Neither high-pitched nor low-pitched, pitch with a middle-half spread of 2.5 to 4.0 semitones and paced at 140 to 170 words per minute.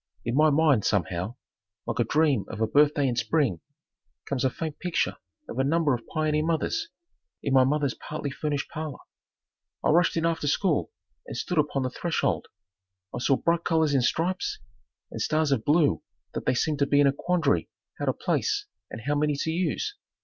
No: medium, 150 Hz; average, 3.1 semitones; average, 190 wpm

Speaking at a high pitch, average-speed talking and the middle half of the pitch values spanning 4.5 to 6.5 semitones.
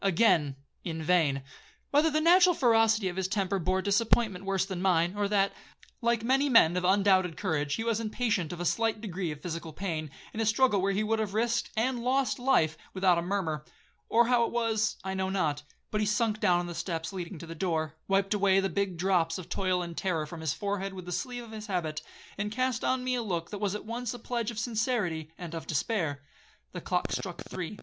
No: high, 195 Hz; fast, 215 wpm; average, 4.8 semitones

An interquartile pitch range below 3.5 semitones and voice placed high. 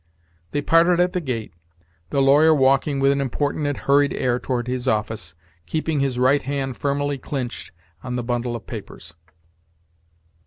No: average, 2.7 semitones; low, 135 Hz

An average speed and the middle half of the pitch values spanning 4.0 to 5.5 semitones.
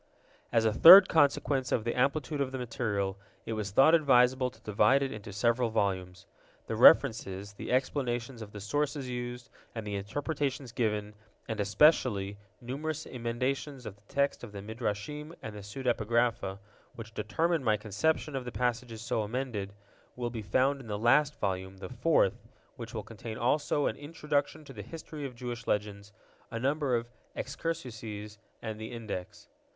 Yes: average, 165 wpm; average, 4.4 semitones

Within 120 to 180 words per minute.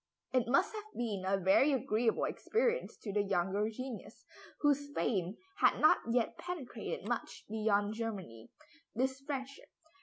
Yes: average, 140 wpm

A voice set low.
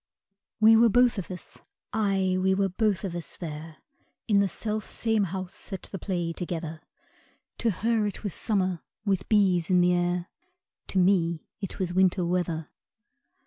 No: medium, 185 Hz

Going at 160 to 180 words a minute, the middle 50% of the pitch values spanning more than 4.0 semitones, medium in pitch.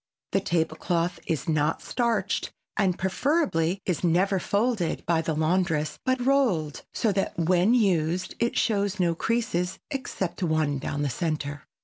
No: average, 145 wpm; average, 4.4 semitones; medium, 180 Hz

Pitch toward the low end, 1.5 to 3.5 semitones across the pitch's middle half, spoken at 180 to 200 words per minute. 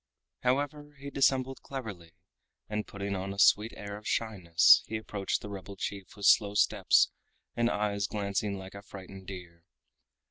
No: low, 100 Hz; narrow, 2.5 semitones; average, 155 wpm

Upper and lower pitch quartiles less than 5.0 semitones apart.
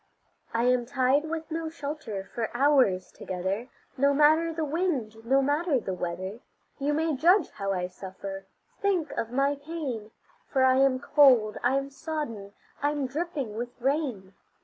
No: wide, 5.4 semitones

